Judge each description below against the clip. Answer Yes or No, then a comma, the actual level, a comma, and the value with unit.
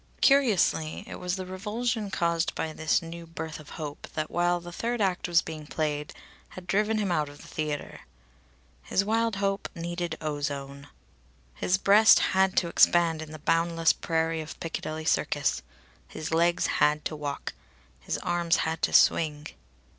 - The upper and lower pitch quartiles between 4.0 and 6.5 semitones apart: No, average, 3.2 semitones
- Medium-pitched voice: Yes, medium, 165 Hz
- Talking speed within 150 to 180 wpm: Yes, average, 160 wpm